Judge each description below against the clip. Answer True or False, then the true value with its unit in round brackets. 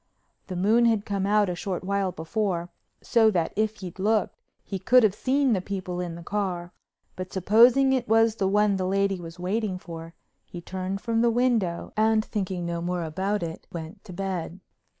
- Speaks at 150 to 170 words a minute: False (190 wpm)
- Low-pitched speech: False (195 Hz)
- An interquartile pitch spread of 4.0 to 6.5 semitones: False (3.5 semitones)